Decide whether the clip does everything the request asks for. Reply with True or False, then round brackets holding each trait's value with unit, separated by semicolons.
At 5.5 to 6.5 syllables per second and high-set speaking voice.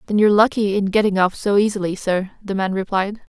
True (5.9 syllables/s; 200 Hz)